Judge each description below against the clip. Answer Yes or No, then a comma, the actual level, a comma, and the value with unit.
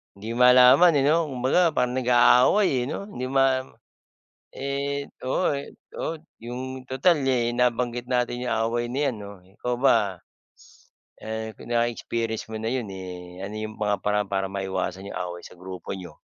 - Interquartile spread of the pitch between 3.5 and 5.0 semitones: Yes, average, 4.2 semitones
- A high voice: No, low, 120 Hz